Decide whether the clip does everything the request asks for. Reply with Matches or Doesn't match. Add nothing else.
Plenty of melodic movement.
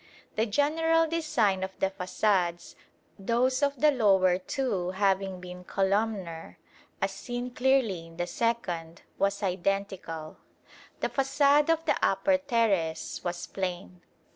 Matches